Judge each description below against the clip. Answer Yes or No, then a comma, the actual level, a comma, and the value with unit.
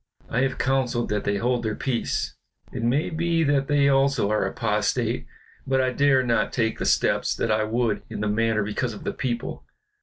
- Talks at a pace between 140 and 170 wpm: No, average, 195 wpm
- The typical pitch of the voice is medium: No, low, 120 Hz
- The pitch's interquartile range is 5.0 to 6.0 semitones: No, average, 3.8 semitones